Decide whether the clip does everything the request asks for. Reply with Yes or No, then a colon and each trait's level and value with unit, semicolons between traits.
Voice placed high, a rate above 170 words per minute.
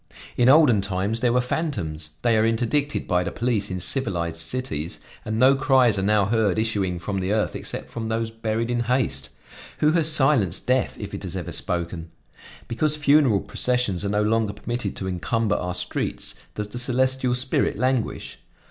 No: low, 115 Hz; average, 180 wpm